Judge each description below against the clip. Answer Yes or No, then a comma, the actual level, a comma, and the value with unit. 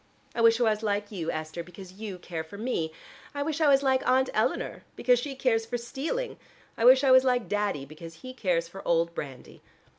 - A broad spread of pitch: Yes, wide, 7.1 semitones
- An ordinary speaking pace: No, fast, 215 wpm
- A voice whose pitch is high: Yes, high, 220 Hz